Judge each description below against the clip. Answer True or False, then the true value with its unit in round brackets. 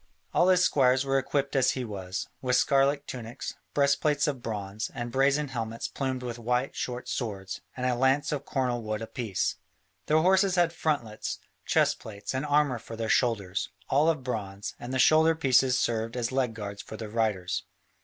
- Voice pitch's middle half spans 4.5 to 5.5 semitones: False (3.9 semitones)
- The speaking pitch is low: True (125 Hz)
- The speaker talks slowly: False (180 wpm)